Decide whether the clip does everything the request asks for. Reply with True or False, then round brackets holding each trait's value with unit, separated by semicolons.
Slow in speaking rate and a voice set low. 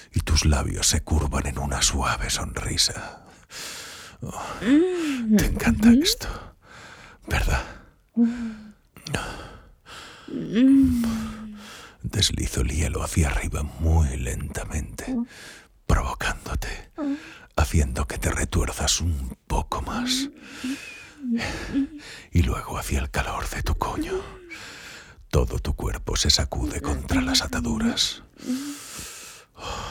True (90 wpm; 110 Hz)